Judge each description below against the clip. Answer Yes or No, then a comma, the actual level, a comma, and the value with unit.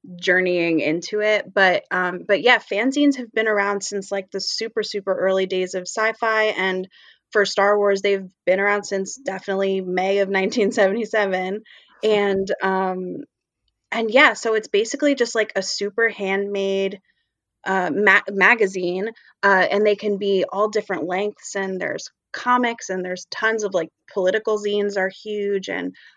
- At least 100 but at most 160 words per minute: Yes, average, 155 wpm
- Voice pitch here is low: No, high, 200 Hz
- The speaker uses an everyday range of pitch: No, narrow, 2.1 semitones